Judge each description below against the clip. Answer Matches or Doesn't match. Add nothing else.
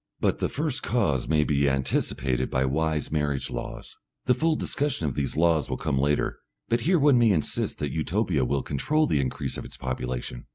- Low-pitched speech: Matches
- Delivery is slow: Doesn't match